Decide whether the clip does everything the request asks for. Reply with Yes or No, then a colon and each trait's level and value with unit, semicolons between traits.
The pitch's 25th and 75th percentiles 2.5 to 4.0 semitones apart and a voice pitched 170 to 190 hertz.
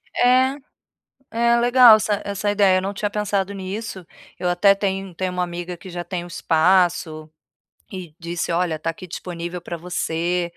Yes: average, 2.8 semitones; medium, 185 Hz